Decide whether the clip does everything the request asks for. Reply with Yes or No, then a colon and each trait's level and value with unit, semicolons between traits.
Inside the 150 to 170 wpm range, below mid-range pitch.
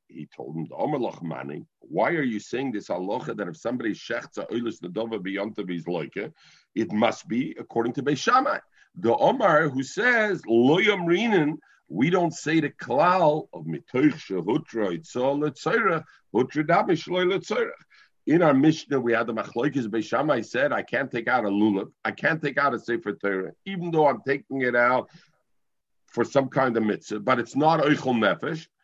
Yes: average, 155 wpm; low, 130 Hz